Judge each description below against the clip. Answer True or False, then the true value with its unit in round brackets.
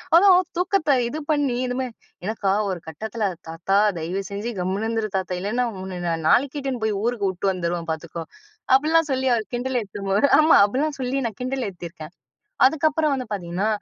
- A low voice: False (220 Hz)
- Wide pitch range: True (6.1 semitones)